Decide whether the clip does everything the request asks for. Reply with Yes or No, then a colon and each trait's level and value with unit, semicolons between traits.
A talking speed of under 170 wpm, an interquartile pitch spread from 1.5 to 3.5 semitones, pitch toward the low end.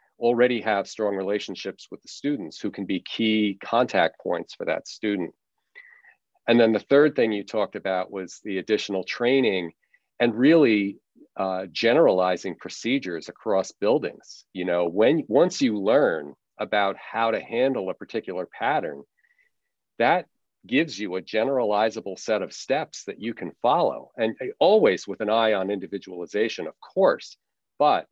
No: average, 150 wpm; average, 4.1 semitones; low, 105 Hz